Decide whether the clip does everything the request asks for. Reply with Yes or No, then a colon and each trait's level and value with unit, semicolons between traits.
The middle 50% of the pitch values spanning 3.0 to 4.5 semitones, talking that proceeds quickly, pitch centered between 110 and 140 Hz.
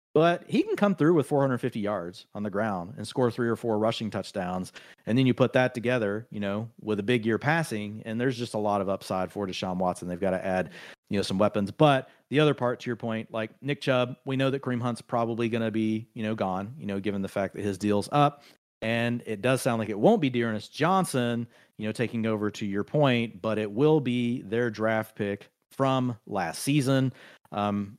Yes: average, 3.7 semitones; fast, 230 wpm; low, 115 Hz